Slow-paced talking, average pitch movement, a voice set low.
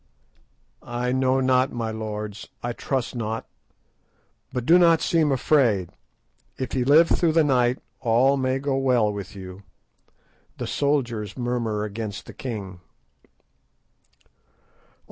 Yes: slow, 125 wpm; average, 3.8 semitones; low, 125 Hz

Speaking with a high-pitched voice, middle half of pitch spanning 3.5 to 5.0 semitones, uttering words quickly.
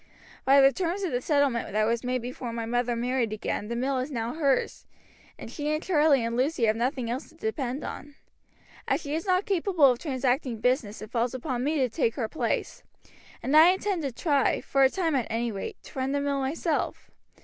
Yes: very high, 265 Hz; average, 4.0 semitones; fast, 215 wpm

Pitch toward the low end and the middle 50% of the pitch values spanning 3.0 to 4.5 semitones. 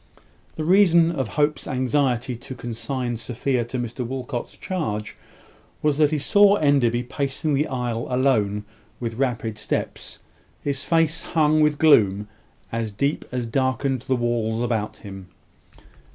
Yes: low, 130 Hz; average, 4.1 semitones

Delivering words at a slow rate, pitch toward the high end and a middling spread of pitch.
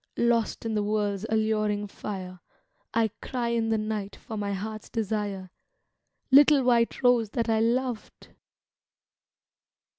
No: slow, 125 wpm; high, 220 Hz; narrow, 2.2 semitones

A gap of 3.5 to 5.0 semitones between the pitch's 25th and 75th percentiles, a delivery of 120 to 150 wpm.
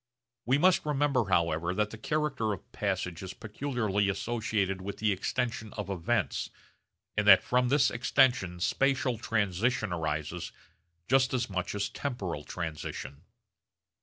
No: wide, 5.4 semitones; slow, 135 wpm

